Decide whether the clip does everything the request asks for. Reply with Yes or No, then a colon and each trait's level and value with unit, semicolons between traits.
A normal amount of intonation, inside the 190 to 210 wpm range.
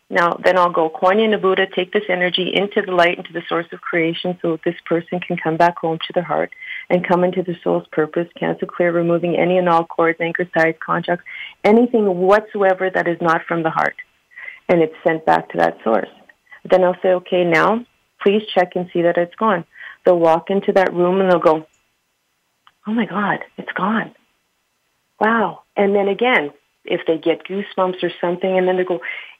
No: narrow, 2.1 semitones; average, 200 wpm